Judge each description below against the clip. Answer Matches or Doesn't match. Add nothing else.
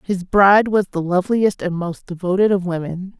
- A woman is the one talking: Matches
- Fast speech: Doesn't match